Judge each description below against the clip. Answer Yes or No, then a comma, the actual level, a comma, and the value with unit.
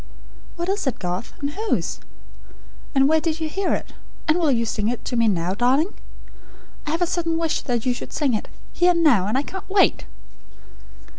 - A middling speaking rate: No, fast, 210 wpm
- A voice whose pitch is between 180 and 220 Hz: No, very high, 295 Hz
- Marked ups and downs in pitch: Yes, wide, 6.2 semitones